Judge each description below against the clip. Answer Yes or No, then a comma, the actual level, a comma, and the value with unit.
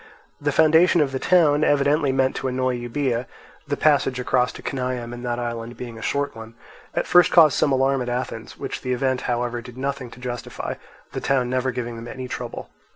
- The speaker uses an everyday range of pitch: No, narrow, 2.3 semitones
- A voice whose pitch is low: Yes, low, 130 Hz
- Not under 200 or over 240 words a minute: Yes, fast, 205 wpm